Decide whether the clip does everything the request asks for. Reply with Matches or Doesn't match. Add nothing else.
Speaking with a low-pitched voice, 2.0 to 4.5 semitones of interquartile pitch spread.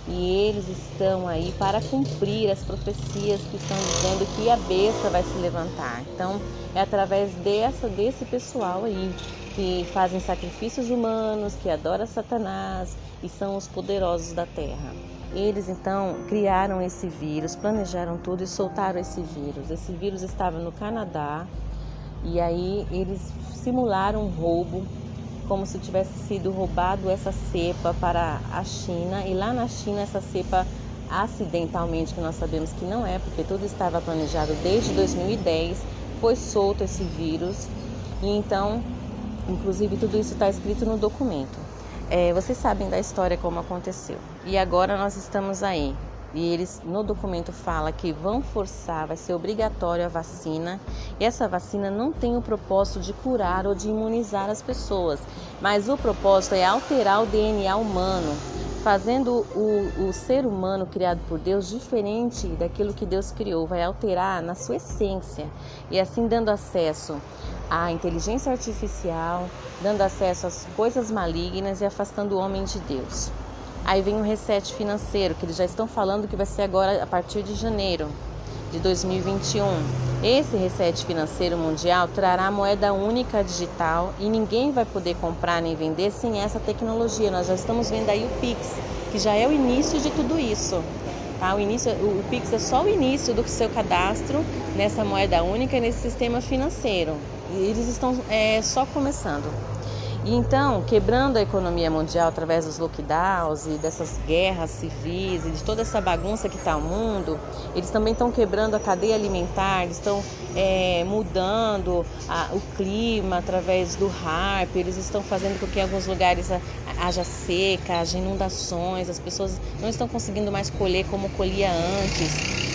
Doesn't match